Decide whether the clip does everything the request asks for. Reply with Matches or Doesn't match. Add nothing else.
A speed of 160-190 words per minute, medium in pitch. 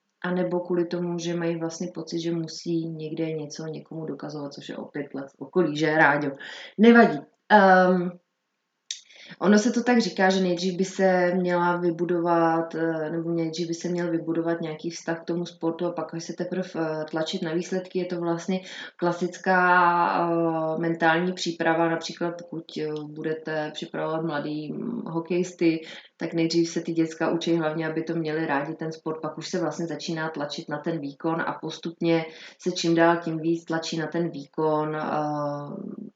Matches